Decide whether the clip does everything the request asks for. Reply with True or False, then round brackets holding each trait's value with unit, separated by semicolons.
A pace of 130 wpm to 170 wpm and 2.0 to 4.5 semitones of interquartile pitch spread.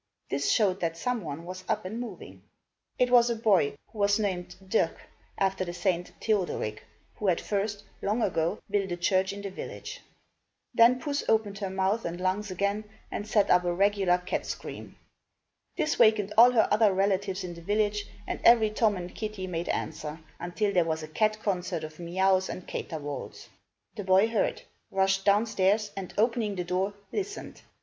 False (180 wpm; 3.1 semitones)